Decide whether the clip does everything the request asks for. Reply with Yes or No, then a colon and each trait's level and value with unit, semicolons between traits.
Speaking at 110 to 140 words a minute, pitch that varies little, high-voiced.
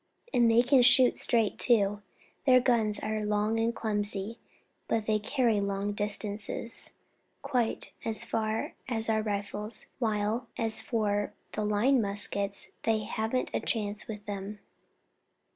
Yes: slow, 135 wpm; narrow, 1.9 semitones; high, 215 Hz